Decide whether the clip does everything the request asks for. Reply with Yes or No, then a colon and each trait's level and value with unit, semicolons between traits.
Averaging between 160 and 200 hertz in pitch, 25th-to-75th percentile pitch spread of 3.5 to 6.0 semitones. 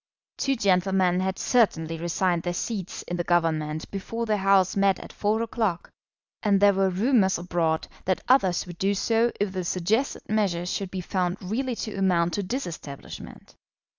No: high, 190 Hz; average, 3.1 semitones